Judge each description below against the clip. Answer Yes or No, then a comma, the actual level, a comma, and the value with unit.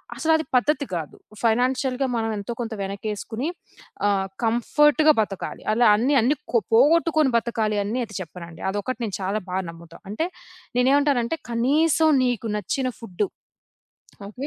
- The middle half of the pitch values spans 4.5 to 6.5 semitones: Yes, average, 5.0 semitones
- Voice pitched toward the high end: Yes, high, 240 Hz